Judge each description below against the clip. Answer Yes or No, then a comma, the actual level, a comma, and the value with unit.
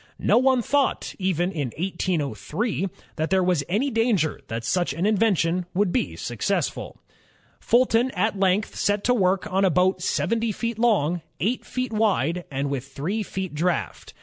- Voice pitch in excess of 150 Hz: Yes, high, 190 Hz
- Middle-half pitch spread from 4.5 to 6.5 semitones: Yes, average, 5.1 semitones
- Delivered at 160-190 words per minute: Yes, average, 170 wpm